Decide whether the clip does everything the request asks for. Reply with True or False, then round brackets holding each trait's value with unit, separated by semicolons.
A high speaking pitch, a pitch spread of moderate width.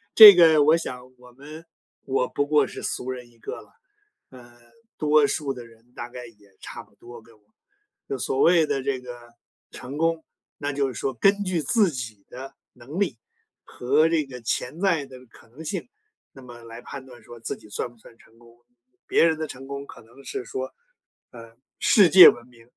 False (130 Hz; 4.3 semitones)